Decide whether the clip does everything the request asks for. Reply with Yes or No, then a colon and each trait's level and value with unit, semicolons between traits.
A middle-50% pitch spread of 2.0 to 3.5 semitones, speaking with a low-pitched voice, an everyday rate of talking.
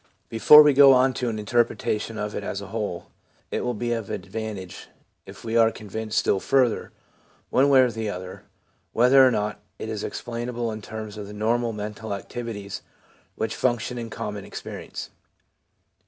Yes: narrow, 2.5 semitones; low, 110 Hz; average, 170 wpm